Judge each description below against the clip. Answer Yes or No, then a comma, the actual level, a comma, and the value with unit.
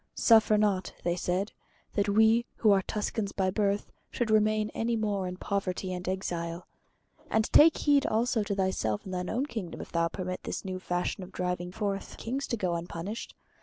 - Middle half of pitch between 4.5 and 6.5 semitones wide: No, average, 3.3 semitones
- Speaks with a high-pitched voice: Yes, high, 200 Hz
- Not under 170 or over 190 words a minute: Yes, average, 185 wpm